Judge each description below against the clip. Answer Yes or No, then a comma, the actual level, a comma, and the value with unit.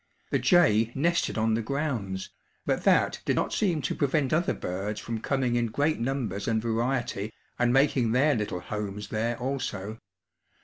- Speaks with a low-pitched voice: Yes, low, 120 Hz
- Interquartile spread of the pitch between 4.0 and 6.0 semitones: Yes, average, 4.3 semitones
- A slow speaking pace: No, average, 165 wpm